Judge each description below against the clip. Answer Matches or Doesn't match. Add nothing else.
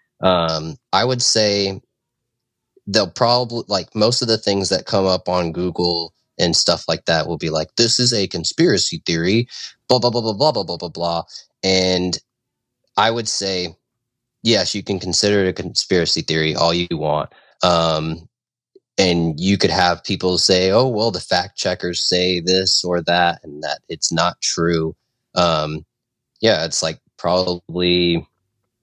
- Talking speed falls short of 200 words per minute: Matches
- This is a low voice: Matches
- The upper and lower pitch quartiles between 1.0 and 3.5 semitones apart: Doesn't match